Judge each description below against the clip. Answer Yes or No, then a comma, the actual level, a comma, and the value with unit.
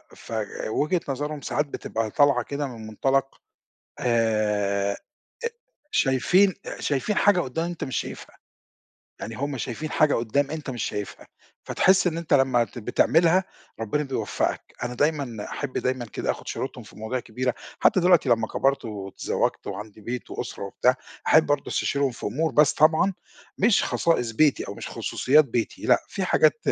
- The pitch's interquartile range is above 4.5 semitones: Yes, average, 5.2 semitones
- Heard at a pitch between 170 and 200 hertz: No, low, 135 Hz